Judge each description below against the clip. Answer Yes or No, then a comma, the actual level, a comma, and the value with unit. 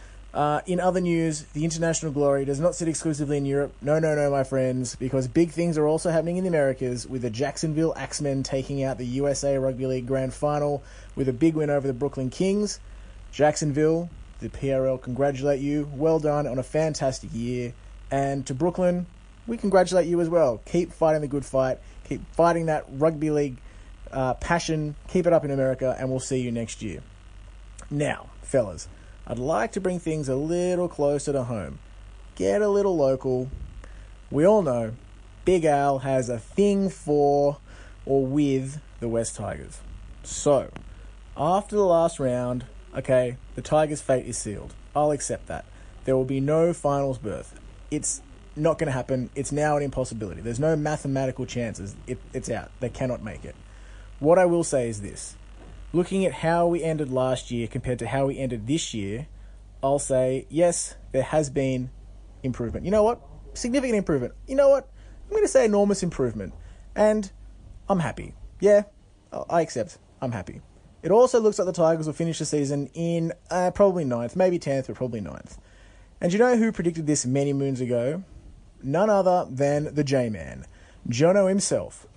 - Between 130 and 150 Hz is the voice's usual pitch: Yes, medium, 140 Hz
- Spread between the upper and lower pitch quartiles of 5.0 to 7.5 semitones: Yes, average, 5.3 semitones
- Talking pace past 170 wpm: Yes, average, 180 wpm